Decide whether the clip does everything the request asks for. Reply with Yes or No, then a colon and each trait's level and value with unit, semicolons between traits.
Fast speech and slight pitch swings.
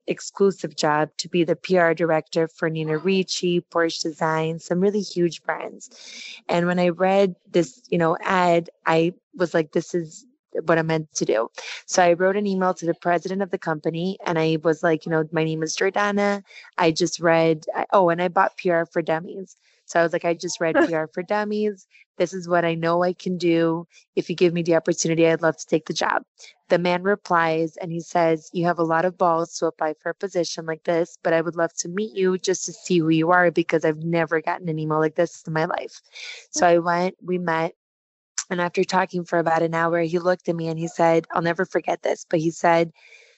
Yes: fast, 225 wpm; narrow, 1.8 semitones